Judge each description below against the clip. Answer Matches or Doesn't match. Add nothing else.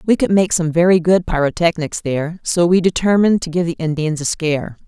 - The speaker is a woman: Matches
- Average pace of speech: Doesn't match